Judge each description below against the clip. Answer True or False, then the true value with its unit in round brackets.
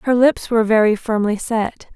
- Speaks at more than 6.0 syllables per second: False (5.1 syllables/s)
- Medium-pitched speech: False (225 Hz)